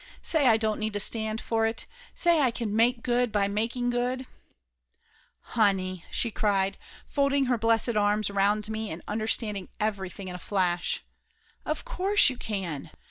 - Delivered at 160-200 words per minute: Yes, average, 170 wpm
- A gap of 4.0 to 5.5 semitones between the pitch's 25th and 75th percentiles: No, average, 3.3 semitones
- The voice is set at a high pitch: Yes, high, 220 Hz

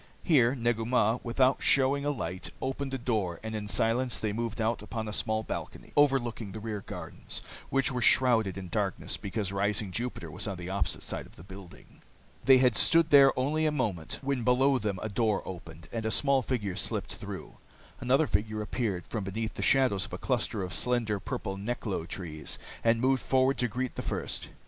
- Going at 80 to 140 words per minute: No, average, 195 wpm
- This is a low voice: Yes, low, 115 Hz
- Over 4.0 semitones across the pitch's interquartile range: Yes, average, 4.4 semitones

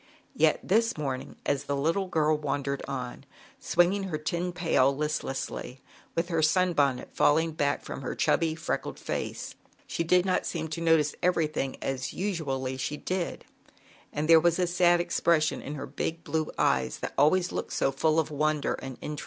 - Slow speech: No, average, 180 wpm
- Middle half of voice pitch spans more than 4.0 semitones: No, average, 3.5 semitones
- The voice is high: No, medium, 155 Hz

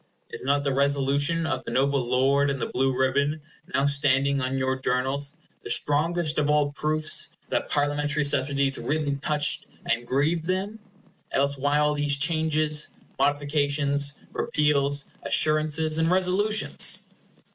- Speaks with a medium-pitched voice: Yes, medium, 145 Hz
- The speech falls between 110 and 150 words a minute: Yes, slow, 135 wpm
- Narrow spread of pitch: Yes, narrow, 1.7 semitones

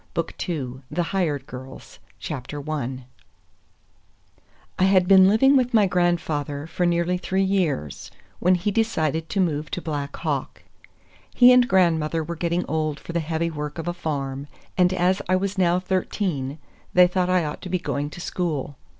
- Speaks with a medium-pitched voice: Yes, medium, 170 Hz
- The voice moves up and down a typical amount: Yes, average, 3.8 semitones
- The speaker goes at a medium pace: Yes, average, 165 wpm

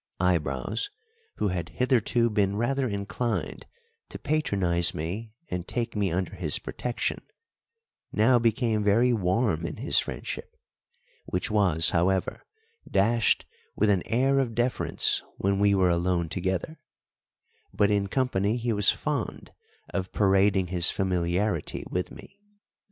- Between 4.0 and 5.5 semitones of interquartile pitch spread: Yes, average, 4.3 semitones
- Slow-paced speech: Yes, slow, 130 wpm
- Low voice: Yes, low, 100 Hz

